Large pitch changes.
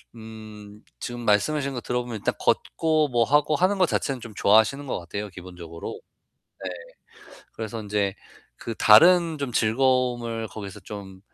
No: average, 4.5 semitones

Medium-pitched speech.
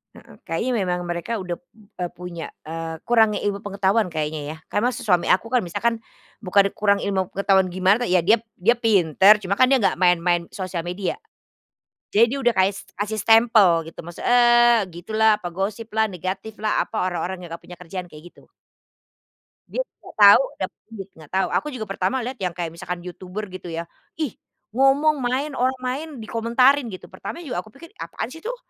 No: high, 200 Hz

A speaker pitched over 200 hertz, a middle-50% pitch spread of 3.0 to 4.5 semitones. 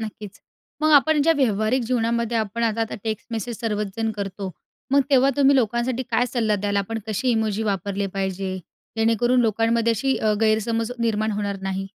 No: high, 225 Hz; narrow, 2.4 semitones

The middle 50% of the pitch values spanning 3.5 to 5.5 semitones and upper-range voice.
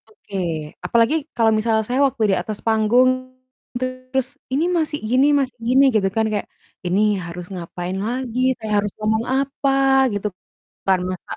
Yes: average, 3.8 semitones; high, 225 Hz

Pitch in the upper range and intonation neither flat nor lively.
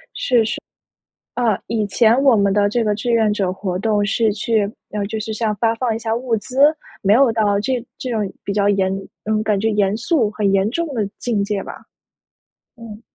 No: high, 215 Hz; narrow, 2.2 semitones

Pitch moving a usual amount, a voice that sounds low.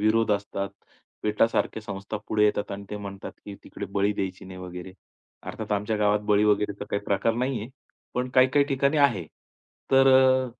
Yes: average, 3.6 semitones; low, 105 Hz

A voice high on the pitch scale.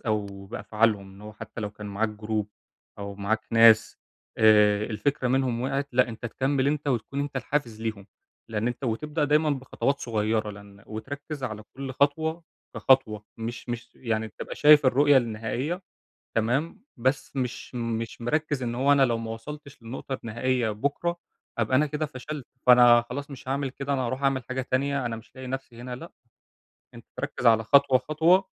No: low, 125 Hz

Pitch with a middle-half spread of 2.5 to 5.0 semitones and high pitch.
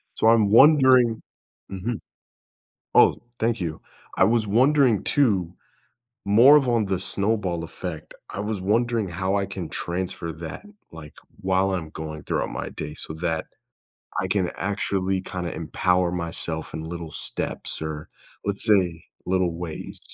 No: average, 4.5 semitones; very low, 95 Hz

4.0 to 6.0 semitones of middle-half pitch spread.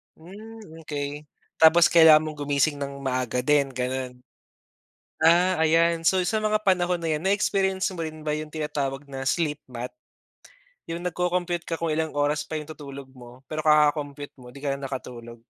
No: average, 3.5 semitones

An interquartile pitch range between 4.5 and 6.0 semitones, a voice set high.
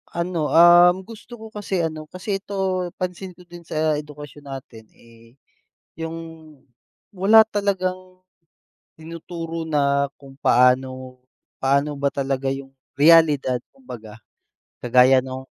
No: average, 5.2 semitones; medium, 155 Hz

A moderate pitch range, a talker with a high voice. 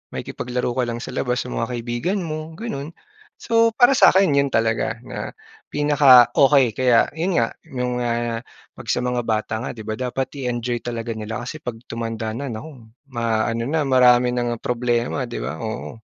No: average, 3.2 semitones; low, 125 Hz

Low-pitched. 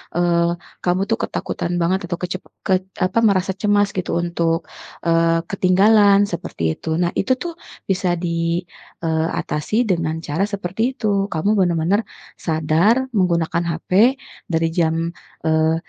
No: medium, 175 Hz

